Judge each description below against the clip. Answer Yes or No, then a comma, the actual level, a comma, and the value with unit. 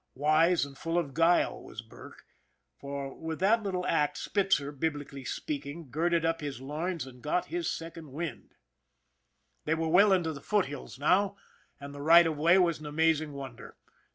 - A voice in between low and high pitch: Yes, medium, 160 Hz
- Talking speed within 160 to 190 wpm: Yes, average, 170 wpm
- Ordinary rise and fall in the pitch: Yes, average, 3.3 semitones